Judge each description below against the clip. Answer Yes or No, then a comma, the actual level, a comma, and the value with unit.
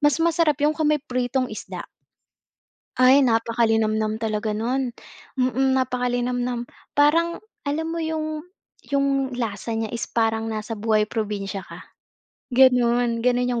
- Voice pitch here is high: Yes, high, 245 Hz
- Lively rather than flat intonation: No, average, 3.8 semitones